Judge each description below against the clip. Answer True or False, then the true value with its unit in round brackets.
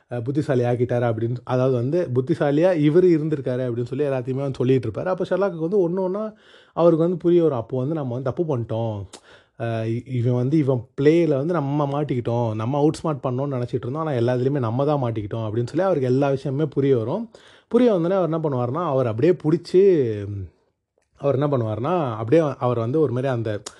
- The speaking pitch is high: False (140 Hz)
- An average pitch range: True (4.9 semitones)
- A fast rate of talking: True (175 wpm)